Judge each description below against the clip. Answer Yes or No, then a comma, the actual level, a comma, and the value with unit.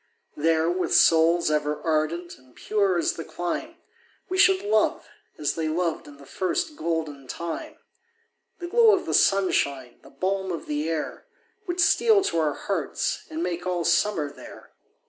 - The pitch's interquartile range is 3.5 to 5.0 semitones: Yes, average, 4.5 semitones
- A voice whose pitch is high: No, medium, 170 Hz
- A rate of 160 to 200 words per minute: Yes, average, 165 wpm